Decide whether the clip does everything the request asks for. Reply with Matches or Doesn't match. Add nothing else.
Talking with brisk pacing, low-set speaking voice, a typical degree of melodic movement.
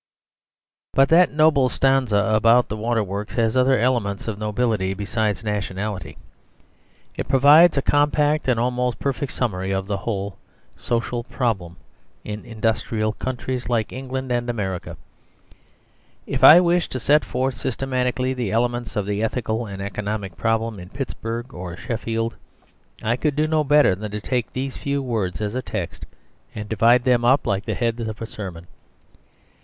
Doesn't match